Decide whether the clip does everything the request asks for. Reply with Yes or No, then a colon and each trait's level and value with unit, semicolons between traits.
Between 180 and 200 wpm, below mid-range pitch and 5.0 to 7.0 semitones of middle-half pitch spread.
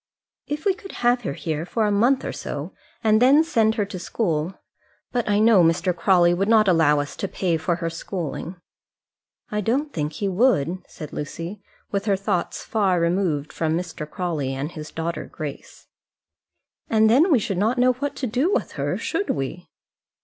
No: average, 185 wpm; high, 190 Hz; wide, 5.4 semitones